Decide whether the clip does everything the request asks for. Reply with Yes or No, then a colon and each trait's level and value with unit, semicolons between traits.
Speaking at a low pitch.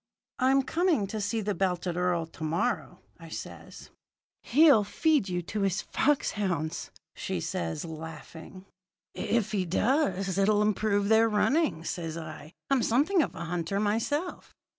No: high, 200 Hz